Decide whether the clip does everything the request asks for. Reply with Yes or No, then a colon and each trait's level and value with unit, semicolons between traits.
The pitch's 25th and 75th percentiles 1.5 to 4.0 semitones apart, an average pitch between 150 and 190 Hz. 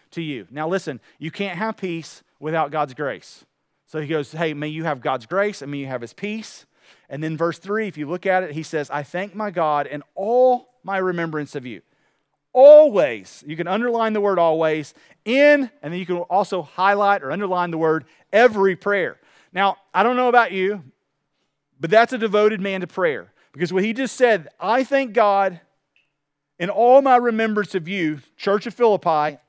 No: average, 5.3 semitones; medium, 185 Hz